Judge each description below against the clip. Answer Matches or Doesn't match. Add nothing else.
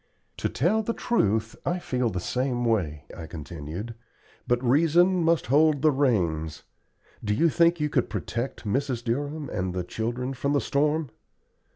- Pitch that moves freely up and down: Matches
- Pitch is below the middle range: Matches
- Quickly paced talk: Doesn't match